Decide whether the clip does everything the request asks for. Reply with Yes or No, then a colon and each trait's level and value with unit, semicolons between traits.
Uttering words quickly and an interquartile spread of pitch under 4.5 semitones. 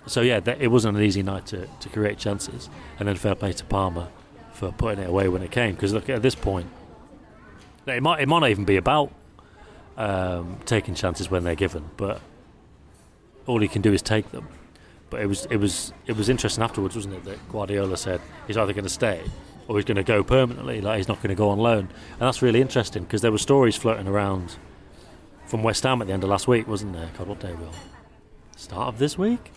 Yes: fast, 230 wpm; average, 3.8 semitones